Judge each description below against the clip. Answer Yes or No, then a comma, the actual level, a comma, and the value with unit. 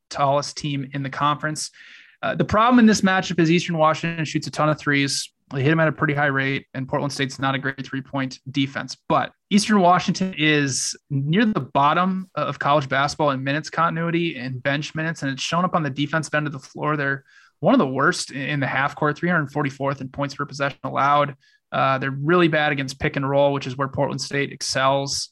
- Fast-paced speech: Yes, fast, 220 wpm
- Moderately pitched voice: Yes, medium, 145 Hz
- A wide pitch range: No, average, 2.7 semitones